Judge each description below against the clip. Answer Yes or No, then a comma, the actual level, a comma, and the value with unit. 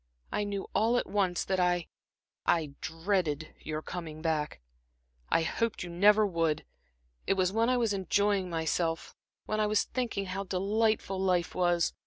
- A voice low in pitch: No, medium, 185 Hz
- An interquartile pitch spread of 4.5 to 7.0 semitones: No, average, 3.7 semitones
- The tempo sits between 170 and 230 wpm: No, average, 160 wpm